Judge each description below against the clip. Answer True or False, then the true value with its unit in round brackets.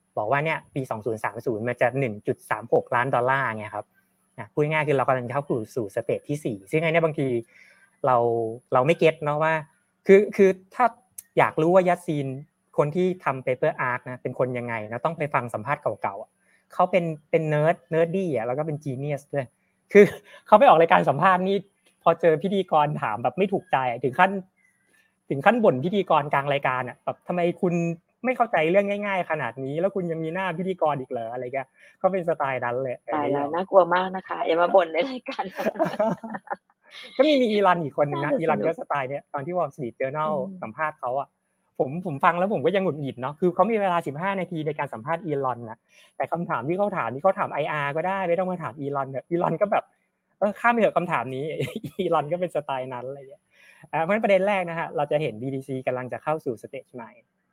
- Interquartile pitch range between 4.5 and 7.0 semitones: True (5.3 semitones)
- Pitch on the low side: False (160 Hz)